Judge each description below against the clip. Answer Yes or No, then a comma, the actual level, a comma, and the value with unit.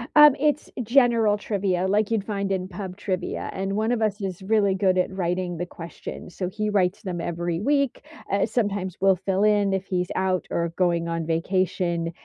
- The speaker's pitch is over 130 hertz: Yes, high, 190 Hz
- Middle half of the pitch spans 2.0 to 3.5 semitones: Yes, narrow, 2.6 semitones